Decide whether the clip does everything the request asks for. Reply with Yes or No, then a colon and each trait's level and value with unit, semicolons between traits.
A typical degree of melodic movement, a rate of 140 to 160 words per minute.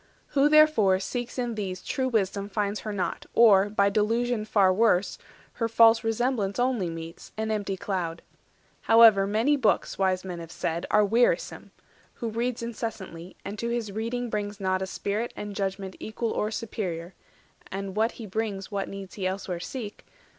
No: average, 3.1 semitones; average, 170 wpm